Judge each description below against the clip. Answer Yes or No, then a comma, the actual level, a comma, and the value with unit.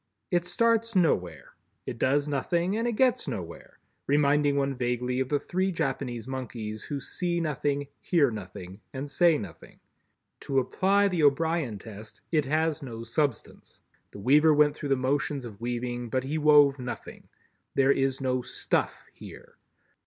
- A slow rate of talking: No, average, 155 wpm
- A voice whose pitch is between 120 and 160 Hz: Yes, medium, 140 Hz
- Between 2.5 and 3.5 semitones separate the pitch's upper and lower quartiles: No, average, 4.4 semitones